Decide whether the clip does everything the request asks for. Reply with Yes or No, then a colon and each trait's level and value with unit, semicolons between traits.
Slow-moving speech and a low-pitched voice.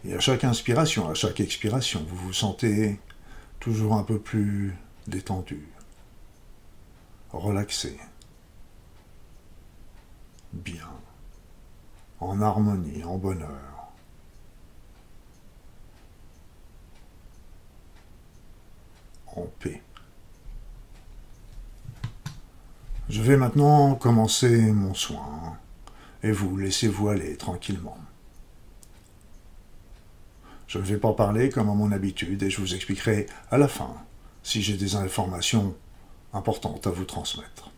Yes: slow, 90 wpm; low, 100 Hz